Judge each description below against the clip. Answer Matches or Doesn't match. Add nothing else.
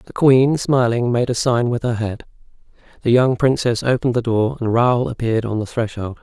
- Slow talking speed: Doesn't match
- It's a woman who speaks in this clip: Doesn't match